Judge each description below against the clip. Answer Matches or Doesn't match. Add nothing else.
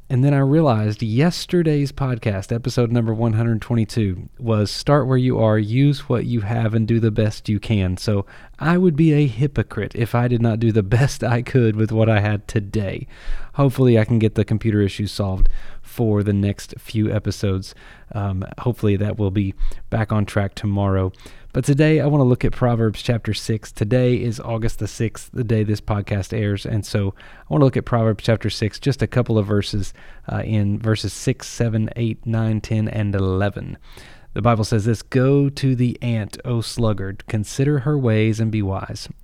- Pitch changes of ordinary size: Matches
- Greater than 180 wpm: Matches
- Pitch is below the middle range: Matches